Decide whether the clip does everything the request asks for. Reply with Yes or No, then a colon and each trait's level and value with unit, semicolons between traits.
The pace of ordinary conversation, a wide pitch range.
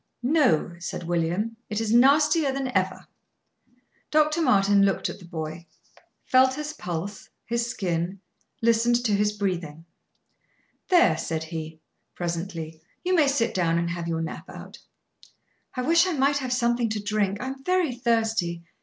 Yes: average, 155 wpm; wide, 7.4 semitones